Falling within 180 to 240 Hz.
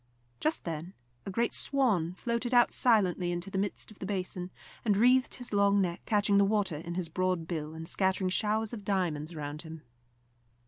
Yes: high, 190 Hz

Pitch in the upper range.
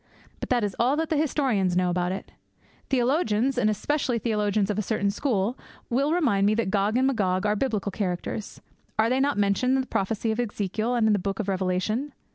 Yes: high, 215 Hz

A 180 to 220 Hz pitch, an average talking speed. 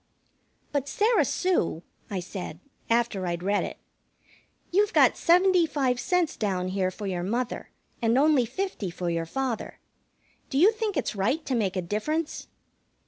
No: high, 240 Hz; average, 155 wpm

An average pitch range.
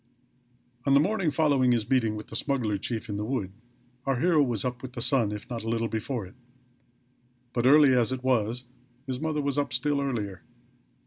Yes: average, 3.8 semitones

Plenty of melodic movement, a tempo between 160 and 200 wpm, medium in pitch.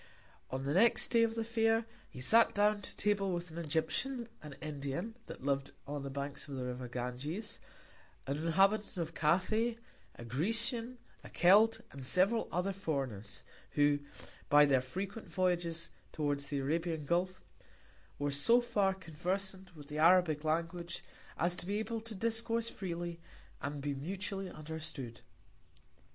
No: wide, 6.0 semitones; average, 150 wpm; medium, 170 Hz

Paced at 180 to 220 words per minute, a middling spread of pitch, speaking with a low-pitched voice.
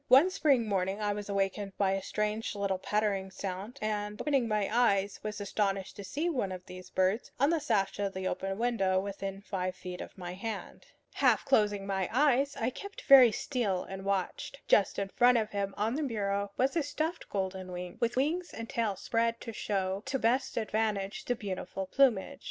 No: average, 195 wpm; average, 3.9 semitones; high, 205 Hz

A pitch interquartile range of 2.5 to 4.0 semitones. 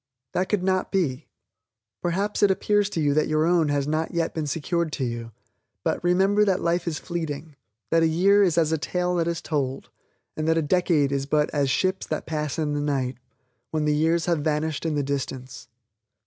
Yes: average, 3.2 semitones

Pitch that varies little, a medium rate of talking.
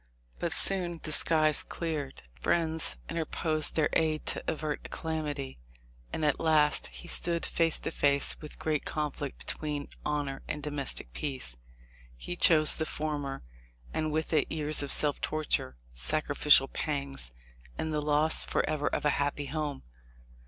Yes: narrow, 1.7 semitones; average, 150 wpm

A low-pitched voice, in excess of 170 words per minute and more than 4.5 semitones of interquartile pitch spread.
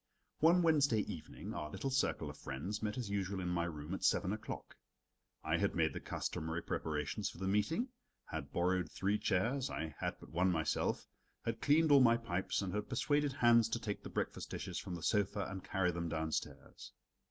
Yes: low, 100 Hz; average, 195 wpm; average, 5.2 semitones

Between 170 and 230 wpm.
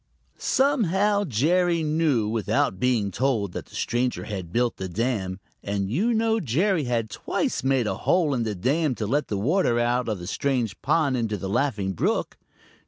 Yes: average, 175 wpm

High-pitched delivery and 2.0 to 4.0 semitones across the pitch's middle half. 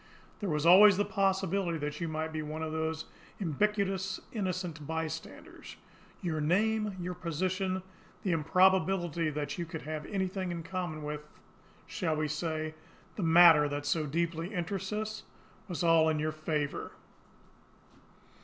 No: medium, 170 Hz; average, 3.3 semitones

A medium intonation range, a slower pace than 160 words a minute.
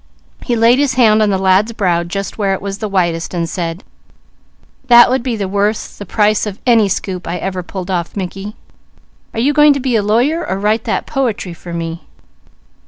No: average, 3.8 semitones; average, 170 wpm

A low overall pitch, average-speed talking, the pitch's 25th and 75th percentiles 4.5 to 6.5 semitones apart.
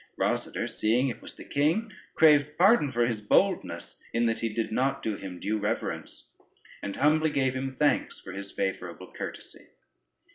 Yes: low, 120 Hz; average, 170 wpm; wide, 5.6 semitones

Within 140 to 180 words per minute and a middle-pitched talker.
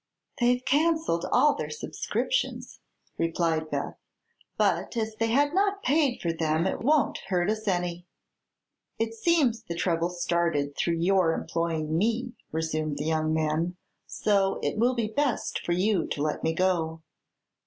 Yes: average, 150 wpm; medium, 180 Hz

